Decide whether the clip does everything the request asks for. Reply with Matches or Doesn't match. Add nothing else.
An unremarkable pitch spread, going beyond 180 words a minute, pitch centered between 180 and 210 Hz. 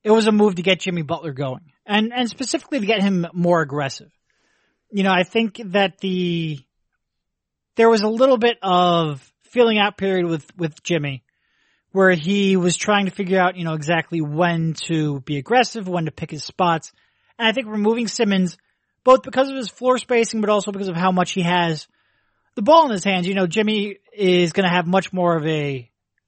Matches